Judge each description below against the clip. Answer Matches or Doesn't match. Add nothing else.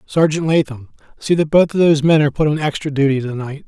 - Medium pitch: Matches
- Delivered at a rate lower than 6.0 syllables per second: Doesn't match